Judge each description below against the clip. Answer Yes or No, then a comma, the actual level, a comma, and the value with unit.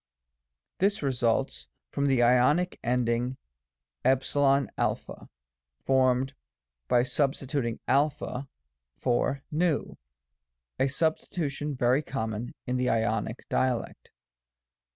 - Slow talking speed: Yes, slow, 85 wpm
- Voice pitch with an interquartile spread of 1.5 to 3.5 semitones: Yes, average, 2.7 semitones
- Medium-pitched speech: No, low, 130 Hz